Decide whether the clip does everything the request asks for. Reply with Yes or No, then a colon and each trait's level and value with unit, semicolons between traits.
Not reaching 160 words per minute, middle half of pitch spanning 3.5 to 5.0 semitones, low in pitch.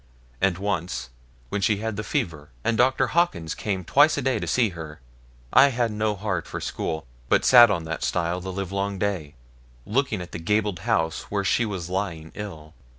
No: average, 190 wpm; average, 4.5 semitones; low, 100 Hz